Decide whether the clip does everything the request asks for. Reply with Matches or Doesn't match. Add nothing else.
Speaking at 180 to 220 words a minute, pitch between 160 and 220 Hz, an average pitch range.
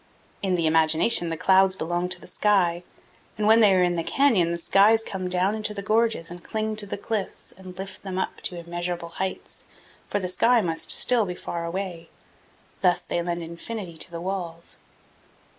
Matches